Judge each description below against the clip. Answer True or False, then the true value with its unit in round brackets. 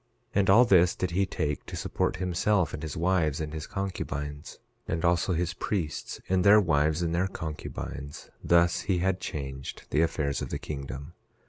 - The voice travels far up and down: False (3.6 semitones)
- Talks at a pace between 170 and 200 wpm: True (185 wpm)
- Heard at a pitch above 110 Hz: False (85 Hz)